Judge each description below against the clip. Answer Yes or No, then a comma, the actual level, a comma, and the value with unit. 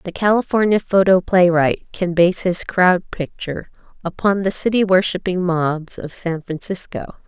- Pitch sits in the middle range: Yes, medium, 180 Hz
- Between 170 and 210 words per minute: No, average, 140 wpm